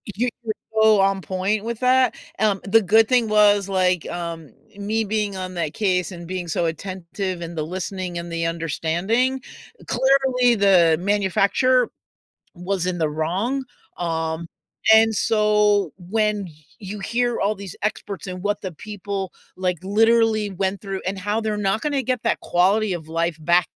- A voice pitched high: Yes, high, 195 Hz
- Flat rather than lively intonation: No, average, 3.6 semitones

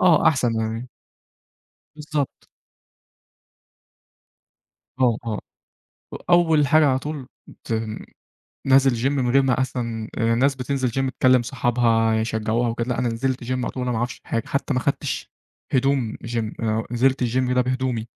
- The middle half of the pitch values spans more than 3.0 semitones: No, narrow, 2.6 semitones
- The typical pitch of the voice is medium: No, low, 125 Hz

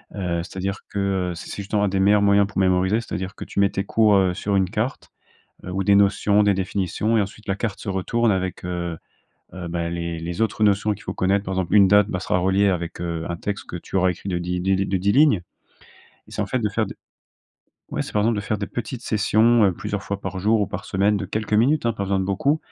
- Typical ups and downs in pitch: No, narrow, 2.1 semitones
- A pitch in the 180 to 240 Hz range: No, low, 100 Hz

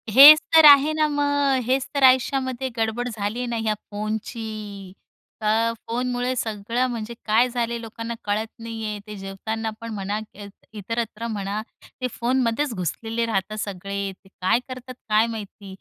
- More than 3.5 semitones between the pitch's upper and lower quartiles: No, average, 3.0 semitones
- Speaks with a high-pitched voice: Yes, high, 225 Hz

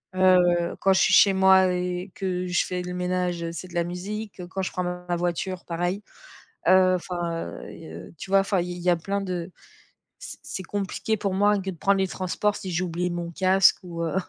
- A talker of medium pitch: Yes, medium, 180 Hz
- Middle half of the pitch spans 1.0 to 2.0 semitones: Yes, narrow, 1.4 semitones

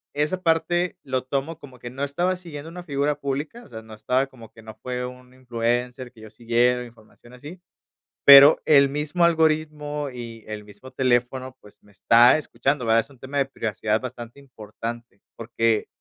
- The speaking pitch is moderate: No, low, 130 Hz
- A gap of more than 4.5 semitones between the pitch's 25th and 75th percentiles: No, average, 3.9 semitones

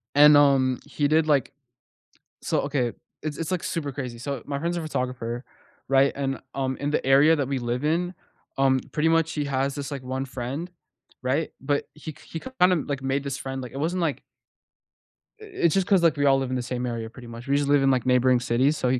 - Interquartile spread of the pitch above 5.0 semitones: No, average, 2.8 semitones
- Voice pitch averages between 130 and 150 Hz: Yes, medium, 140 Hz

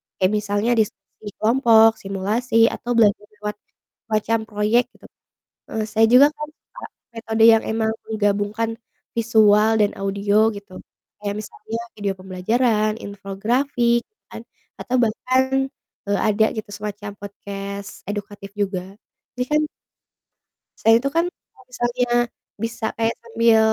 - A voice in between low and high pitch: No, high, 220 Hz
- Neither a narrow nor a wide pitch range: No, narrow, 2.2 semitones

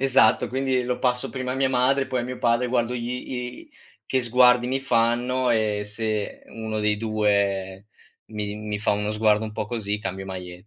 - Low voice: Yes, low, 115 Hz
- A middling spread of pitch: Yes, average, 3.1 semitones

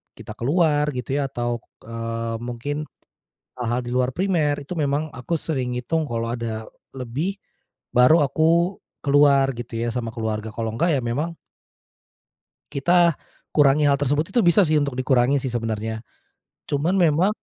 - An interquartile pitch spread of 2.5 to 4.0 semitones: No, average, 4.5 semitones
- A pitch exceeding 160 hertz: No, low, 135 Hz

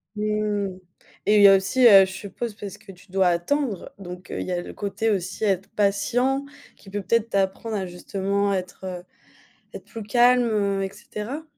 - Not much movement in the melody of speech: Yes, narrow, 2.2 semitones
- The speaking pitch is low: No, high, 200 Hz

